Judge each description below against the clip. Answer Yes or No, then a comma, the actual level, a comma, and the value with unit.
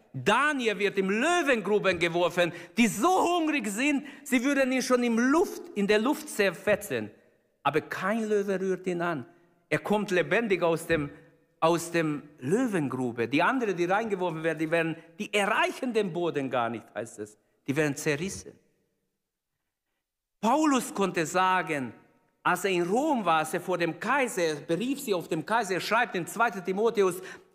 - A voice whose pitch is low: No, high, 190 Hz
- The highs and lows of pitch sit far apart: Yes, wide, 6.1 semitones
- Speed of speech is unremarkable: Yes, average, 165 wpm